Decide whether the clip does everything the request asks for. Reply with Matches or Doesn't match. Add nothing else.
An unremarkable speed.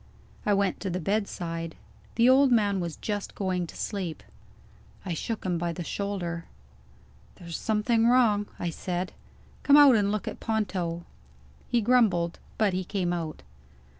Matches